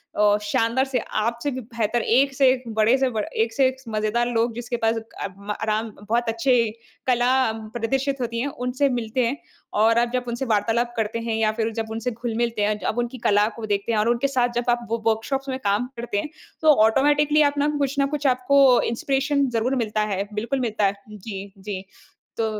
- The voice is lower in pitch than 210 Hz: No, high, 235 Hz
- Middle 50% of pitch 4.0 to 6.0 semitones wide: No, average, 2.8 semitones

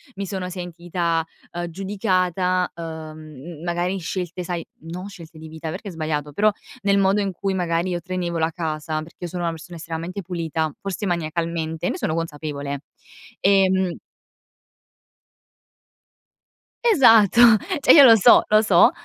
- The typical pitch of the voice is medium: Yes, medium, 175 Hz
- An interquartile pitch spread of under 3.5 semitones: Yes, average, 2.8 semitones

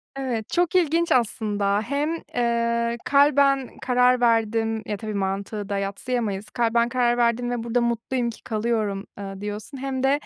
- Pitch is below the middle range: No, high, 235 Hz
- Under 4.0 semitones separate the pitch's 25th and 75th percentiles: Yes, average, 3.1 semitones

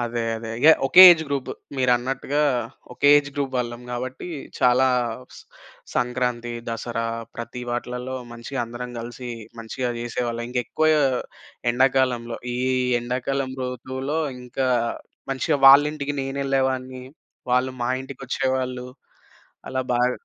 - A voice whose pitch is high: No, low, 125 Hz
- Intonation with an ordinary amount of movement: No, narrow, 1.8 semitones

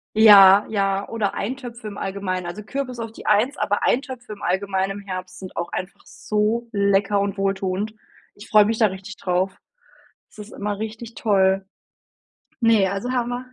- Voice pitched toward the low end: No, high, 205 Hz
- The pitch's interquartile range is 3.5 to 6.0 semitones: No, narrow, 2.5 semitones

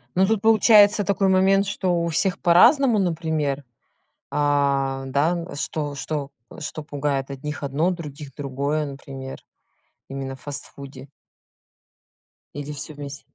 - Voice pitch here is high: No, medium, 150 Hz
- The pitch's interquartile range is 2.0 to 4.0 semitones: No, average, 4.6 semitones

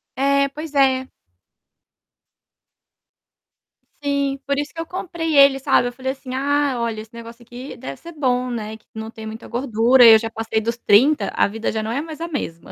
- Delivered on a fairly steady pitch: No, average, 3.8 semitones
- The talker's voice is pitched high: Yes, very high, 255 Hz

